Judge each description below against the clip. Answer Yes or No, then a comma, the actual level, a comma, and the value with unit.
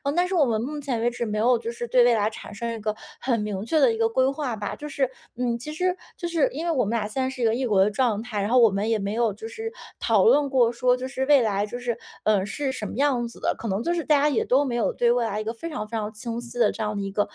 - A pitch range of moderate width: Yes, average, 3.7 semitones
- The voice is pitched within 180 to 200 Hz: No, high, 235 Hz